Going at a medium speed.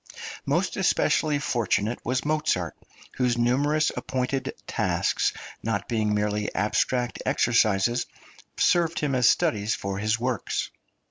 No: slow, 115 wpm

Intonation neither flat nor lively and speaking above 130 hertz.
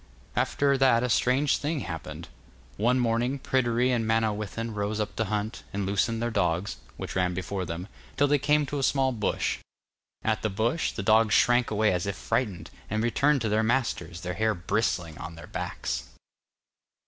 No: average, 3.8 semitones; low, 110 Hz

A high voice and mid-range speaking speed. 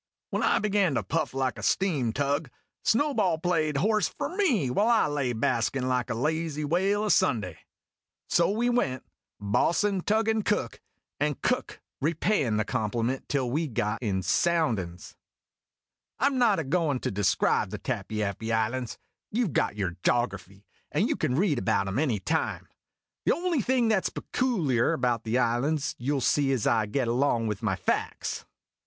No: medium, 140 Hz; average, 175 wpm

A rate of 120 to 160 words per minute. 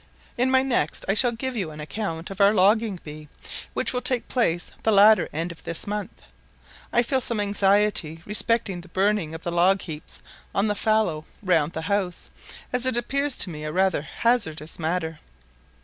No: average, 185 wpm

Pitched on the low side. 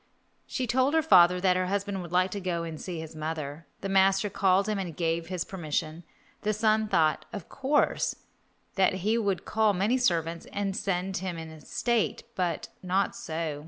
No: medium, 185 Hz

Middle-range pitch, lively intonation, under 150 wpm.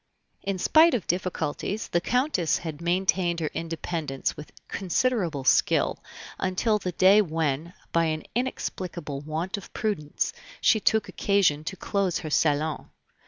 No: medium, 175 Hz; average, 4.2 semitones; slow, 135 wpm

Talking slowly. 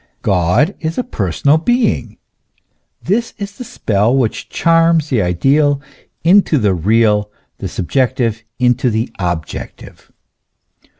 Yes: slow, 115 wpm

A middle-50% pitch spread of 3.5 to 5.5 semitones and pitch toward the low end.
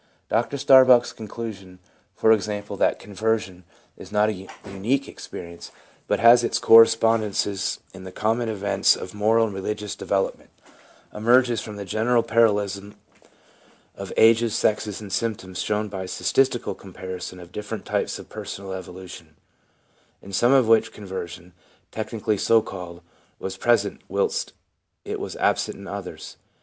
No: average, 3.1 semitones; low, 105 Hz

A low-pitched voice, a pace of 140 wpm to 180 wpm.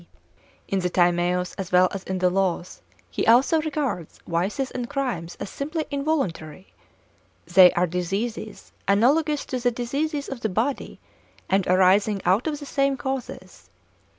No: high, 215 Hz; average, 150 wpm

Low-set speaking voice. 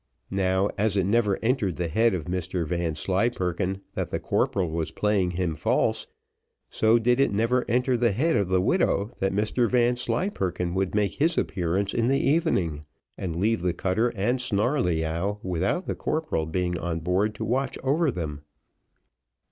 Yes: low, 100 Hz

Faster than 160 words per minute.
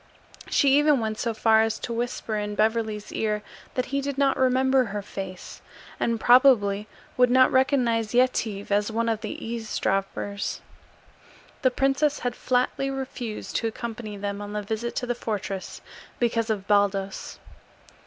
No: average, 155 wpm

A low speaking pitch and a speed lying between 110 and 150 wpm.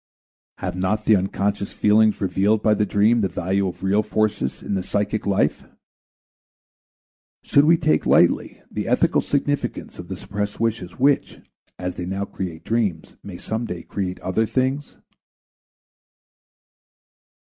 Yes: low, 100 Hz; average, 140 wpm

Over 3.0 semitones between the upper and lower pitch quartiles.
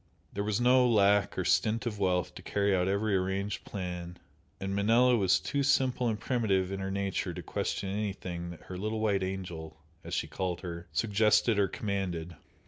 No: average, 2.7 semitones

